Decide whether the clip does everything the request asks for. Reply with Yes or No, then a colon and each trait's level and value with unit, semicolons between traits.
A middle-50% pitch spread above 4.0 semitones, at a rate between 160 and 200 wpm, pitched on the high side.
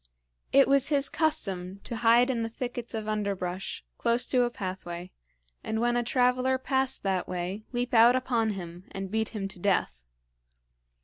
Yes: average, 4.4 semitones; average, 170 wpm; high, 225 Hz